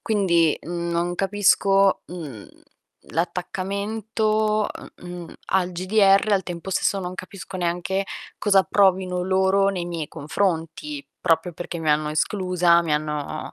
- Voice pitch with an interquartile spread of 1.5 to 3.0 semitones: Yes, narrow, 2.5 semitones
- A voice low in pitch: No, medium, 180 Hz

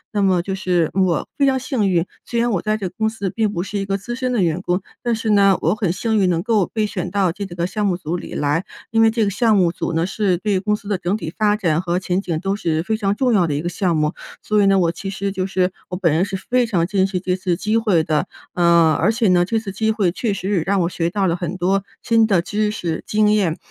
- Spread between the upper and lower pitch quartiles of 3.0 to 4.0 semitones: Yes, average, 3.4 semitones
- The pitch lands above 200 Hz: No, high, 195 Hz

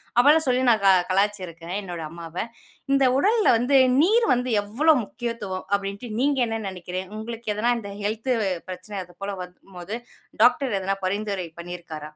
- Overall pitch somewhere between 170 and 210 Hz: Yes, high, 205 Hz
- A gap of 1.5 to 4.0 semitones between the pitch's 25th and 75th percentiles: No, average, 5.2 semitones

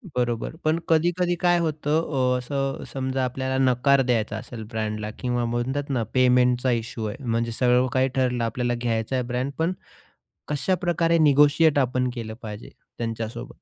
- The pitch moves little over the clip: No, average, 3.3 semitones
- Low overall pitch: Yes, low, 125 Hz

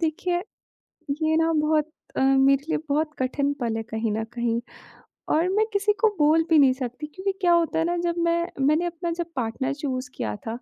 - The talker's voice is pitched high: Yes, very high, 300 Hz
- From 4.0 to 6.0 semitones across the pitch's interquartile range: Yes, average, 4.7 semitones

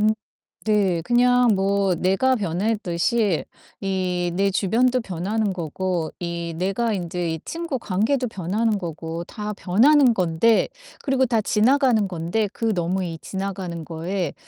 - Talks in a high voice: Yes, high, 195 Hz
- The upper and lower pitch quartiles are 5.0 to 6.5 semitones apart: No, average, 4.4 semitones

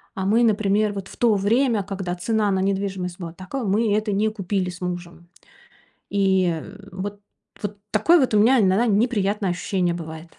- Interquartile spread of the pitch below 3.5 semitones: Yes, average, 2.7 semitones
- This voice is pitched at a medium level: No, high, 200 Hz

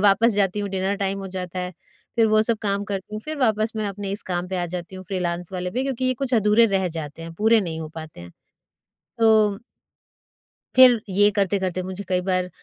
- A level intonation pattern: No, average, 3.0 semitones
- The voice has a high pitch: Yes, high, 195 Hz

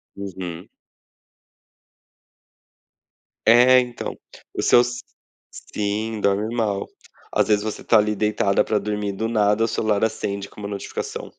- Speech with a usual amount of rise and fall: No, narrow, 1.8 semitones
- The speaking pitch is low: Yes, low, 105 Hz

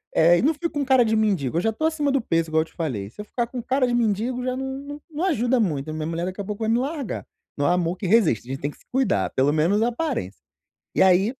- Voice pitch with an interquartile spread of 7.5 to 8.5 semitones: Yes, wide, 7.8 semitones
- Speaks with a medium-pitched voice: No, high, 215 Hz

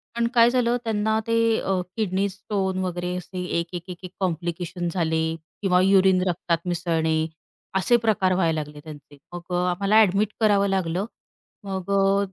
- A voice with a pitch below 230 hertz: Yes, medium, 185 Hz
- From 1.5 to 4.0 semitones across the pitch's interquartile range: Yes, narrow, 2.4 semitones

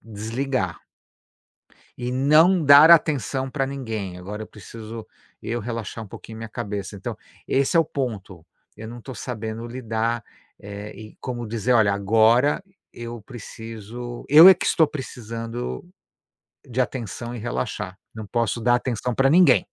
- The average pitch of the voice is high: No, low, 115 Hz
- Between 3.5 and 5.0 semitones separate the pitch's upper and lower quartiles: No, average, 3.1 semitones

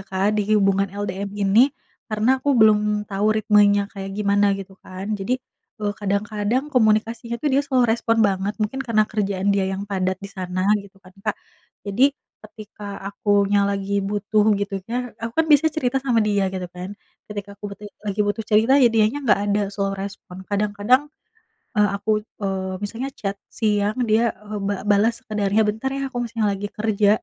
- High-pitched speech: Yes, high, 205 Hz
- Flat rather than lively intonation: Yes, narrow, 1.8 semitones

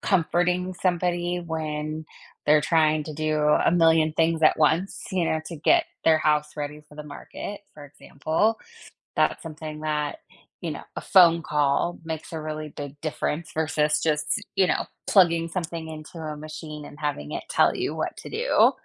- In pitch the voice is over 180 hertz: No, medium, 155 Hz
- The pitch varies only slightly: Yes, narrow, 1.8 semitones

